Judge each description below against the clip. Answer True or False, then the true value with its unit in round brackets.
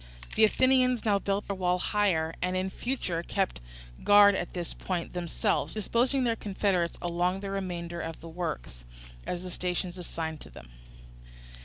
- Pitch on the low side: False (185 Hz)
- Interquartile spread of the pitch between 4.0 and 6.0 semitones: False (3.0 semitones)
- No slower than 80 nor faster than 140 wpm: False (160 wpm)